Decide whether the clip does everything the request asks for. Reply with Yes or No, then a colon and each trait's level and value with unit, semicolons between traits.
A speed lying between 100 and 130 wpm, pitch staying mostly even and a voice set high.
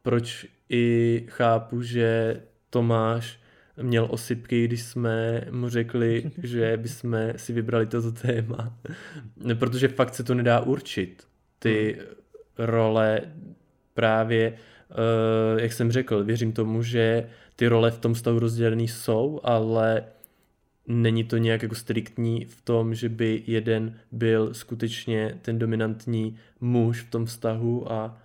No: average, 125 wpm; narrow, 0.9 semitones; low, 115 Hz